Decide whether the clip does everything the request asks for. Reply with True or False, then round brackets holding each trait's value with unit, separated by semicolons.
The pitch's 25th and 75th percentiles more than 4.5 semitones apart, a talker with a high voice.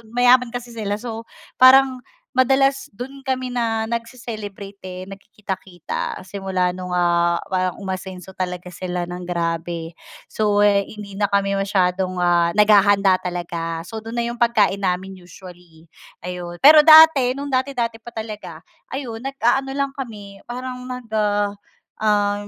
True (5.1 semitones; 205 Hz)